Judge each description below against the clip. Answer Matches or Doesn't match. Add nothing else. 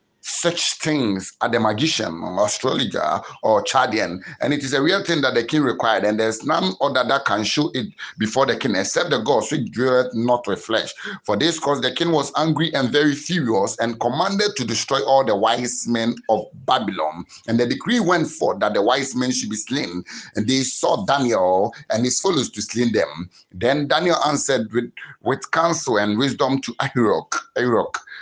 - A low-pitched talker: Matches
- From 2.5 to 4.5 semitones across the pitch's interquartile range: Doesn't match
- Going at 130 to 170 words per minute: Doesn't match